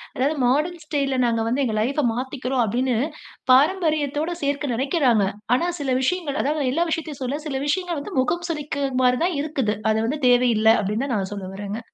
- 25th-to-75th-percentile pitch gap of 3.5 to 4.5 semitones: Yes, average, 3.8 semitones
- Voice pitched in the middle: No, very high, 270 Hz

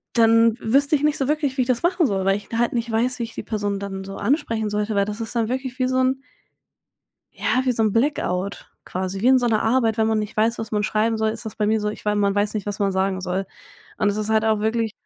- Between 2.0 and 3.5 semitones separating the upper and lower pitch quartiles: Yes, average, 2.8 semitones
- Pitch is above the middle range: Yes, high, 220 Hz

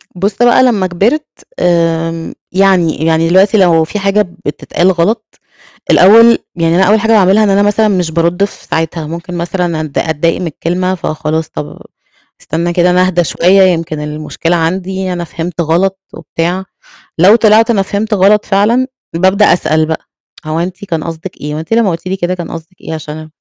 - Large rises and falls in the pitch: No, average, 3.1 semitones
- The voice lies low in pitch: No, medium, 180 Hz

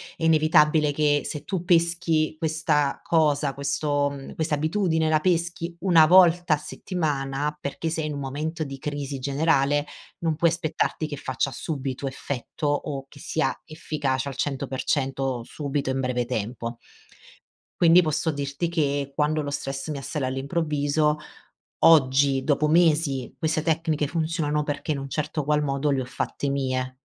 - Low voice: No, medium, 150 Hz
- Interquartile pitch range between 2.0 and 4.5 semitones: Yes, narrow, 2.6 semitones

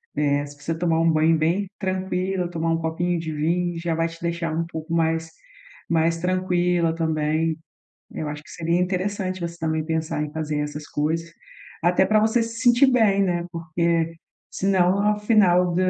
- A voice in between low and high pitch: Yes, medium, 170 Hz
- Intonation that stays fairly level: Yes, narrow, 2.3 semitones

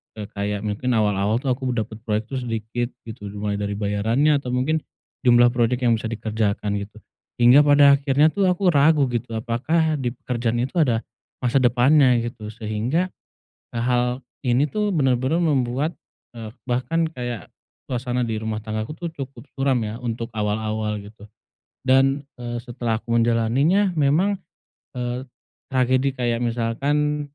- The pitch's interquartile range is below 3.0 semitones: No, average, 3.8 semitones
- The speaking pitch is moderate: No, low, 120 Hz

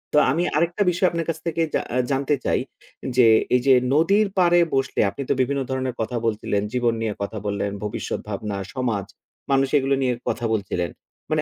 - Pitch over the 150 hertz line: No, low, 130 Hz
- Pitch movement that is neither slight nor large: No, wide, 6.0 semitones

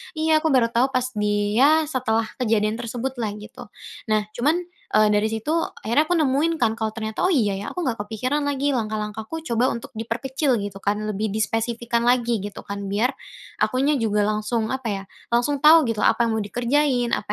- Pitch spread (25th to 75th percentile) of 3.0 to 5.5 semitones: Yes, average, 3.7 semitones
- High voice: Yes, high, 235 Hz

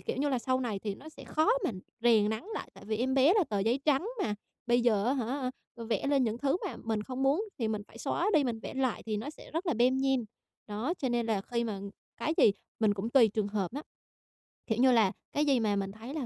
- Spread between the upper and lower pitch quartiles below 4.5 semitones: Yes, average, 3.9 semitones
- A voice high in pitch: Yes, high, 240 Hz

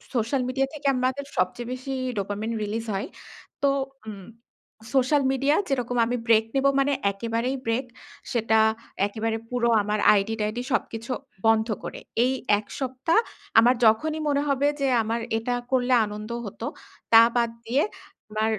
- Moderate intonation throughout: Yes, average, 3.2 semitones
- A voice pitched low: No, high, 235 Hz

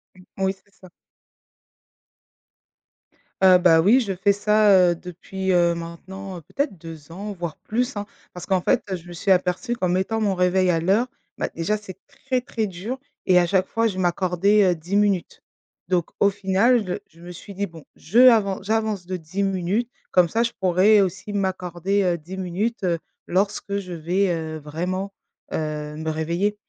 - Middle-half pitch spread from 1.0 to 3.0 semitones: Yes, average, 2.7 semitones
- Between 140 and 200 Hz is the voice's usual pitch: Yes, high, 190 Hz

